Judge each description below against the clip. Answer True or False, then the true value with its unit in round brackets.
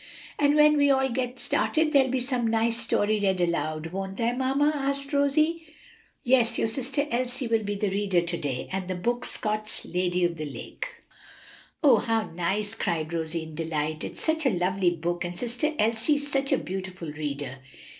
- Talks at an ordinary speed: True (185 wpm)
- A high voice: True (215 Hz)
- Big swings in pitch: True (7.0 semitones)